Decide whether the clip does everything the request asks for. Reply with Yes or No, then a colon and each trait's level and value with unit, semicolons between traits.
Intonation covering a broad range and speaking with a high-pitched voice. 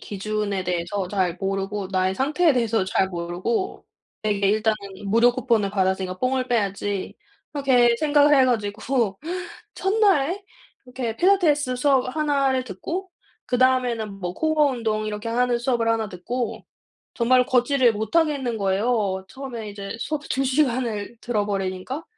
No: average, 4.8 semitones; high, 235 Hz